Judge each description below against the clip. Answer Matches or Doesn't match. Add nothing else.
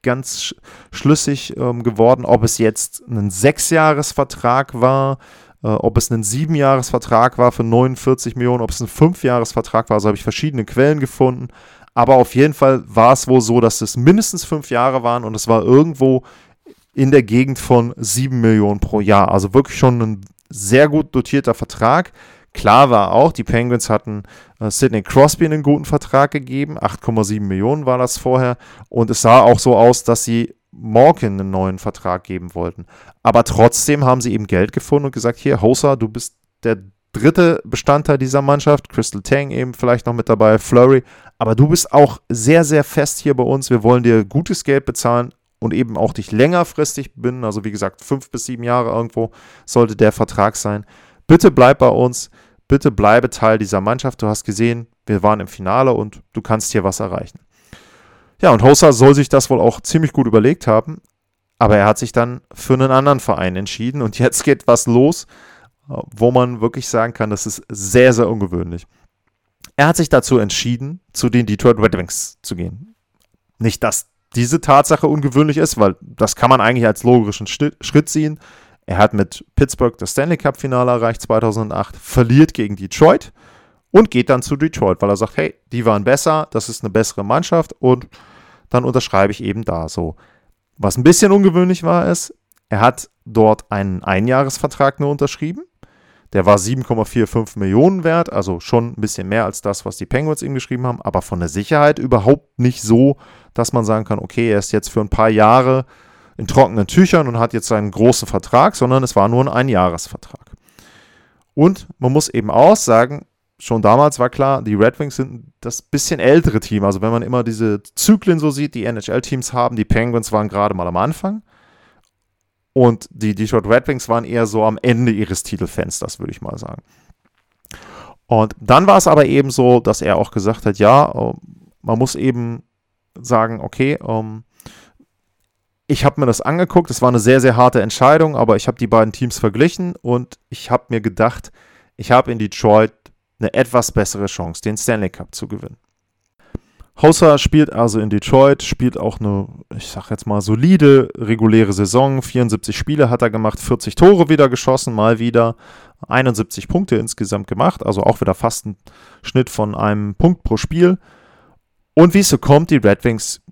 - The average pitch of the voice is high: Doesn't match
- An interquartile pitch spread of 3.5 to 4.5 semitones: Matches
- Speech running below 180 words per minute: Doesn't match